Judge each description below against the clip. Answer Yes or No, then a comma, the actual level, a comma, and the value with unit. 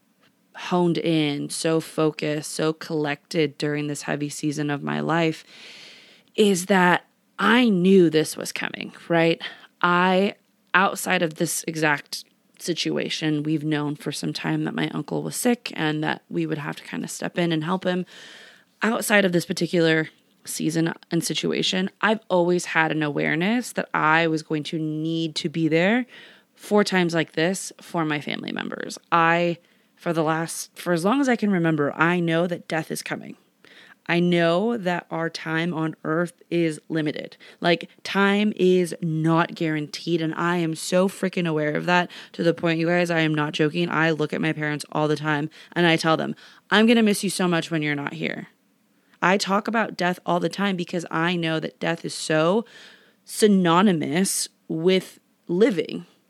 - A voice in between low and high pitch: Yes, medium, 170 Hz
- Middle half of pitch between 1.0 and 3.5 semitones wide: Yes, average, 3.0 semitones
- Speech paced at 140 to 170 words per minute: No, average, 180 wpm